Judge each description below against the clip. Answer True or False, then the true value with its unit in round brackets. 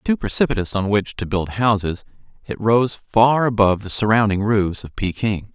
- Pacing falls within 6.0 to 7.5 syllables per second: False (5.0 syllables/s)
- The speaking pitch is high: False (105 Hz)